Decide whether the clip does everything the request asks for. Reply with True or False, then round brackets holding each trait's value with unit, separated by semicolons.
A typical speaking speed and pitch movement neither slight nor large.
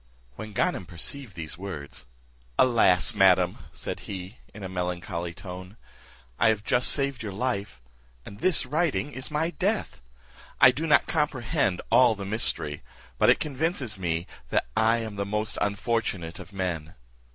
False (150 wpm; 5.9 semitones)